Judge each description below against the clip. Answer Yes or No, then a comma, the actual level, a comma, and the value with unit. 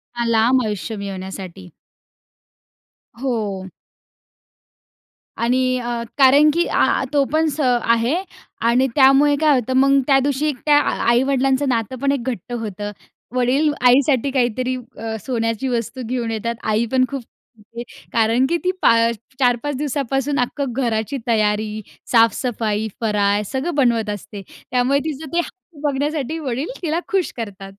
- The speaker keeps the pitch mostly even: No, average, 3.6 semitones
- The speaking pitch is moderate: No, very high, 250 Hz